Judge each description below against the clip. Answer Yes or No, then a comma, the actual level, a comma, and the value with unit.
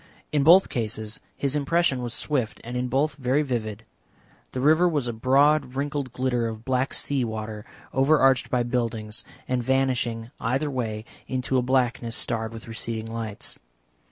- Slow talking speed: No, average, 155 wpm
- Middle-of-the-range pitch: No, low, 125 Hz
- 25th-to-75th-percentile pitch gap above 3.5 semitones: No, average, 3.1 semitones